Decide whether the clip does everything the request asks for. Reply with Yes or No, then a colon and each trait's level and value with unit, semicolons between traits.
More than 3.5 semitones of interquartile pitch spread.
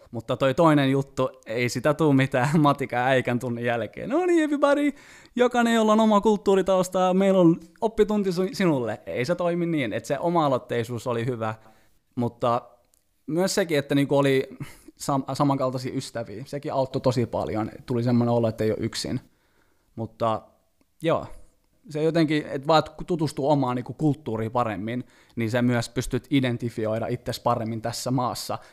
Yes: wide, 5.6 semitones